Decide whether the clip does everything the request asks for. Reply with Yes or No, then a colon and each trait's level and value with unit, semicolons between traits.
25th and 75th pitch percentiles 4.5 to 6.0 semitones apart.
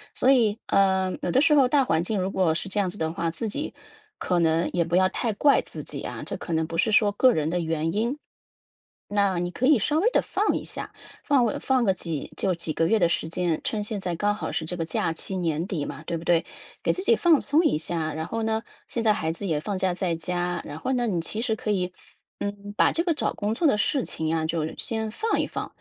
Yes: average, 5.2 semitones